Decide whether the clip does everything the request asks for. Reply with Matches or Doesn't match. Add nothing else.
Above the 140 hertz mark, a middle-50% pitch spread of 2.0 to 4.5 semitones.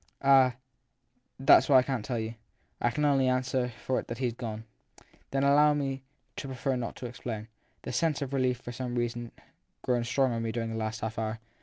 Doesn't match